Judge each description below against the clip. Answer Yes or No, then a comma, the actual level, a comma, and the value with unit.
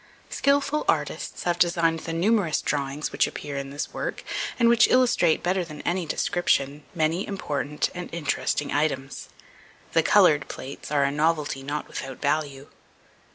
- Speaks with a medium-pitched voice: Yes, medium, 155 Hz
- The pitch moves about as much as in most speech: Yes, average, 3.6 semitones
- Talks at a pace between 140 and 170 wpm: Yes, average, 150 wpm